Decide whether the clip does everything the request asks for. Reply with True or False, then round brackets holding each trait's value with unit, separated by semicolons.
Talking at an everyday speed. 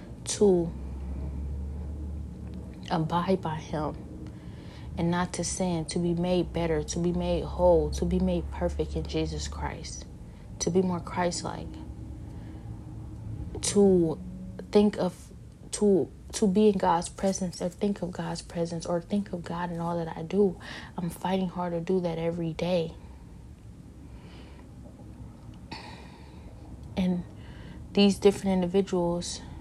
False (130 wpm)